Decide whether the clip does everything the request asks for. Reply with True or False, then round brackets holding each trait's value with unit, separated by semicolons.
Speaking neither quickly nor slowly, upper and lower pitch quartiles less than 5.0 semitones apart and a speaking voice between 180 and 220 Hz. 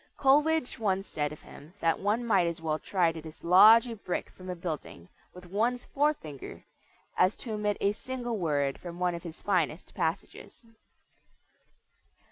False (160 wpm; 5.4 semitones; 185 Hz)